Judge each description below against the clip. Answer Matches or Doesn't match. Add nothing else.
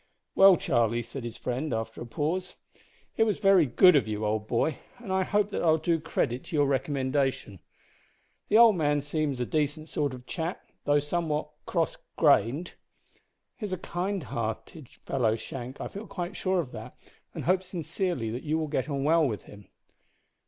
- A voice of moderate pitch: Matches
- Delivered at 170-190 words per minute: Matches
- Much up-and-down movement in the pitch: Matches